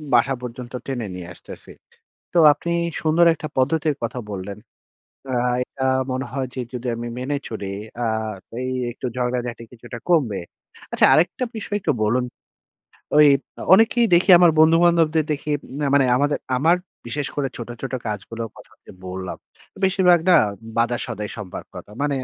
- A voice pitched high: No, low, 130 Hz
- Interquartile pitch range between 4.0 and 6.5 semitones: Yes, average, 5.3 semitones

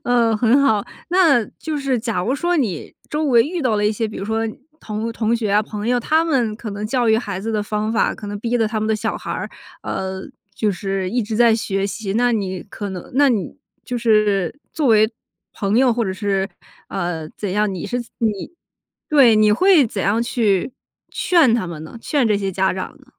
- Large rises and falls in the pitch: No, average, 3.3 semitones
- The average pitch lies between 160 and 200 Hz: No, high, 220 Hz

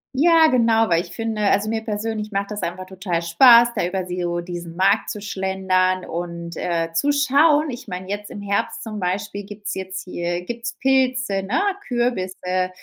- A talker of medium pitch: No, high, 200 Hz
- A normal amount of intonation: Yes, average, 3.9 semitones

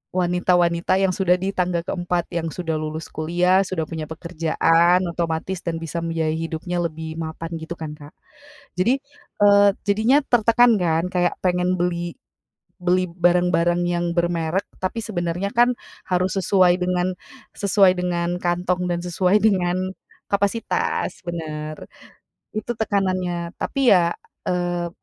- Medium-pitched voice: Yes, medium, 175 Hz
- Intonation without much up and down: Yes, narrow, 1.7 semitones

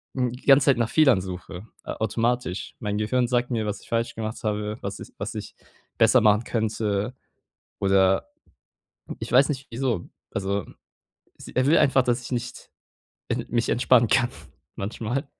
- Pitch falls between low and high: No, low, 115 Hz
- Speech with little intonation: No, average, 3.1 semitones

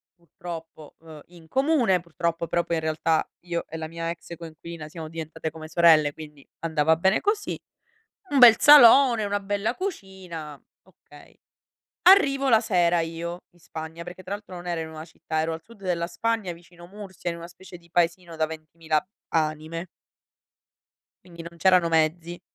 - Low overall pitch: No, medium, 170 Hz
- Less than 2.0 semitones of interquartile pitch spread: No, average, 2.7 semitones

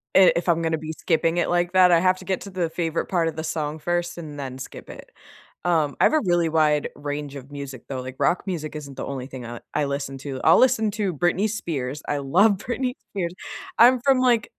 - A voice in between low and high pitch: Yes, medium, 165 Hz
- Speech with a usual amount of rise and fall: Yes, average, 4.4 semitones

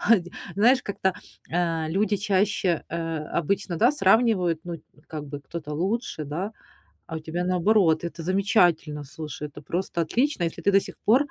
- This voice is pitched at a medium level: Yes, medium, 175 Hz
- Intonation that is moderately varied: Yes, average, 3.8 semitones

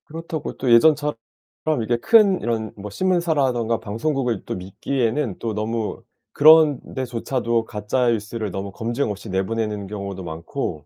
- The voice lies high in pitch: No, low, 115 Hz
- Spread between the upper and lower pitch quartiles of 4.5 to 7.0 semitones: Yes, average, 5.1 semitones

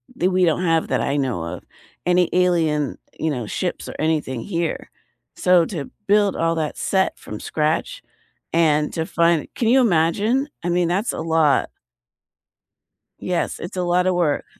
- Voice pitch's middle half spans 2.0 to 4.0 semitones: Yes, average, 2.7 semitones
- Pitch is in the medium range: Yes, medium, 170 Hz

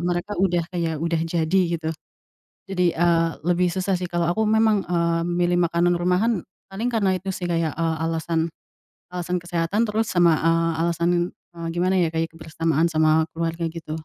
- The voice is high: No, medium, 170 Hz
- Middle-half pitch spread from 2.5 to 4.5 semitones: No, narrow, 1.6 semitones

